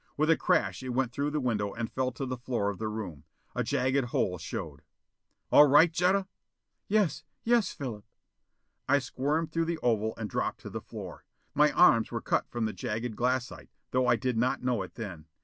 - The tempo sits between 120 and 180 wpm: No, average, 200 wpm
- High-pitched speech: No, low, 125 Hz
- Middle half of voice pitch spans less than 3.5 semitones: No, average, 4.9 semitones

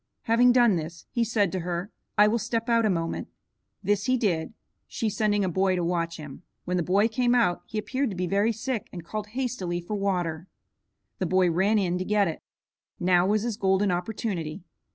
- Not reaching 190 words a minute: No, fast, 205 wpm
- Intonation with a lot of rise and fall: No, average, 4.0 semitones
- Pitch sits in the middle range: No, high, 195 Hz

